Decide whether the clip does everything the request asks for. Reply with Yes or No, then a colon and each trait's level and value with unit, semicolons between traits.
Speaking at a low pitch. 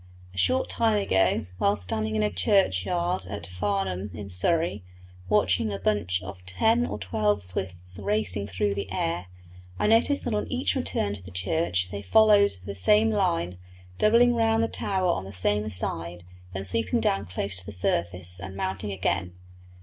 Yes: low, 100 Hz